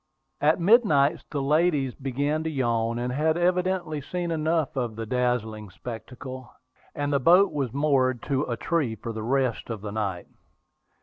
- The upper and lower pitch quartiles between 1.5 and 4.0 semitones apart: No, average, 4.7 semitones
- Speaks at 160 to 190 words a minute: Yes, average, 165 wpm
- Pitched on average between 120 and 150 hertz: Yes, low, 135 Hz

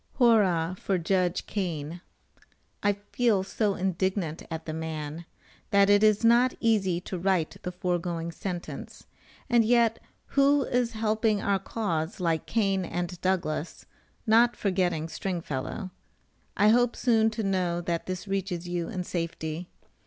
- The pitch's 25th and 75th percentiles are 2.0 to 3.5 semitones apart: No, average, 4.1 semitones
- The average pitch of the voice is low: No, high, 190 Hz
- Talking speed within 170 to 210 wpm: No, average, 140 wpm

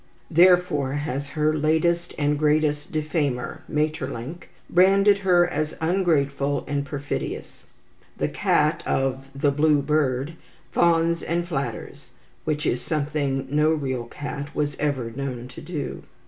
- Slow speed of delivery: Yes, slow, 125 wpm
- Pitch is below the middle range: No, medium, 150 Hz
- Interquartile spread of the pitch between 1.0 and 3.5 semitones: Yes, average, 2.7 semitones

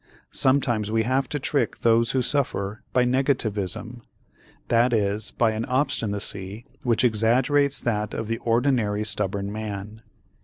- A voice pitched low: Yes, low, 115 Hz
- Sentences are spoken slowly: Yes, slow, 130 wpm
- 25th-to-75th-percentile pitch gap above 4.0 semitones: No, average, 3.3 semitones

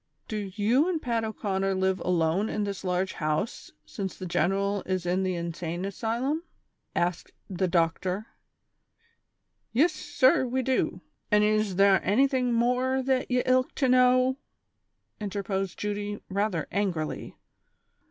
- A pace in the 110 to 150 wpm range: Yes, average, 145 wpm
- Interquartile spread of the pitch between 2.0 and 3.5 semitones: No, average, 5.0 semitones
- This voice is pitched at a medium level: No, high, 205 Hz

